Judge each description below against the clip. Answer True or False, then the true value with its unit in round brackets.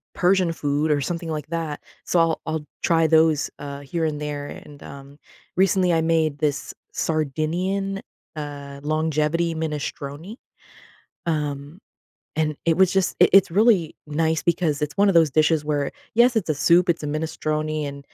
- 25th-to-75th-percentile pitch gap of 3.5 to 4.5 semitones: False (2.4 semitones)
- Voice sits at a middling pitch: True (155 Hz)